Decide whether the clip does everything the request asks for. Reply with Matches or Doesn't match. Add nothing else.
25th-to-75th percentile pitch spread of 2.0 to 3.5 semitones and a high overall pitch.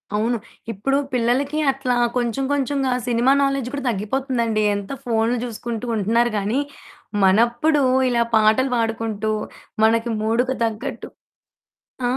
Matches